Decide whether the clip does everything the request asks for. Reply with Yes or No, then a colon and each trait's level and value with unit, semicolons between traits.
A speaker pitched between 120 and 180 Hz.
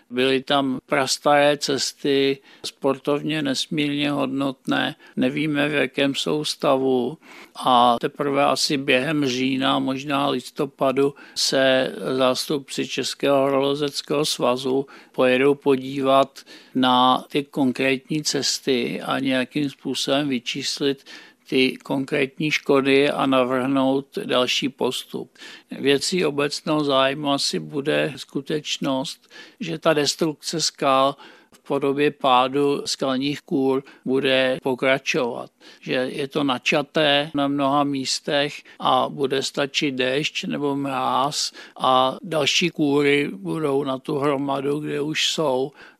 Yes: medium, 140 Hz